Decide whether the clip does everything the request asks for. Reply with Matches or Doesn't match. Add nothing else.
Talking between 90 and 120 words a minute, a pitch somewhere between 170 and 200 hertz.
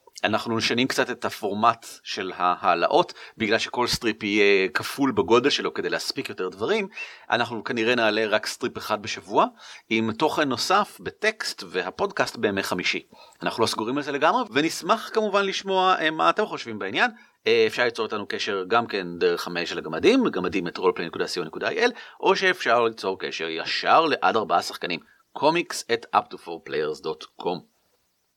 Doesn't match